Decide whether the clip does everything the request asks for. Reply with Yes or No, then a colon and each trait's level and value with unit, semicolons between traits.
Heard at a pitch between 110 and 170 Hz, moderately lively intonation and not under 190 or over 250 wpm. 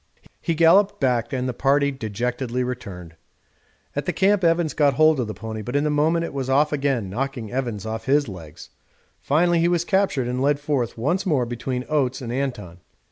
Yes: low, 135 Hz; average, 4.2 semitones; average, 195 wpm